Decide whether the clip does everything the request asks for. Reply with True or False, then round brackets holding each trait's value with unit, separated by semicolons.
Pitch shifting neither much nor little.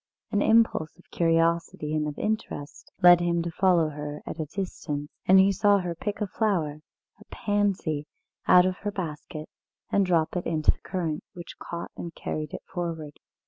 True (3.6 semitones)